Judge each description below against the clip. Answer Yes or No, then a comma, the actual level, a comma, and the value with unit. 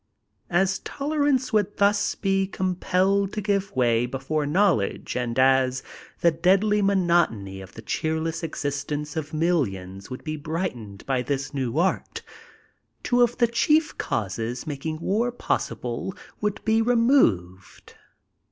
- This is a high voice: No, medium, 160 Hz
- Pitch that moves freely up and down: Yes, wide, 7.7 semitones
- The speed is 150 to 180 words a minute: No, slow, 135 wpm